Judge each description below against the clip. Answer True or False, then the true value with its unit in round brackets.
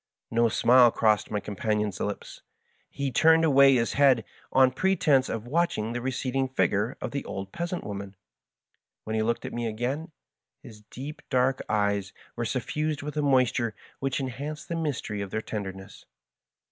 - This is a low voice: True (125 Hz)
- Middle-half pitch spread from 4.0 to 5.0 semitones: True (4.7 semitones)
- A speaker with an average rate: True (170 wpm)